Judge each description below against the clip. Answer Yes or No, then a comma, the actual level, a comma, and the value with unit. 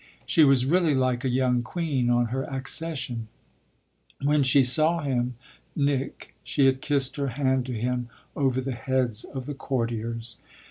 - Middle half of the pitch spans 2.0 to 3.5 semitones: Yes, narrow, 2.4 semitones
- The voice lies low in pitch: Yes, low, 130 Hz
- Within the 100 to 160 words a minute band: Yes, average, 155 wpm